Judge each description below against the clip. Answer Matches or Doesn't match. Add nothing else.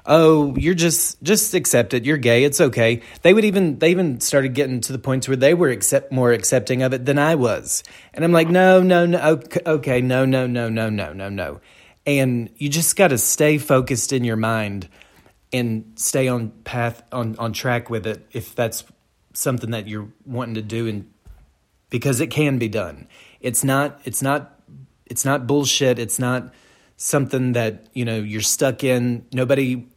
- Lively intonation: Doesn't match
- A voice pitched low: Matches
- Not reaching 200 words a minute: Matches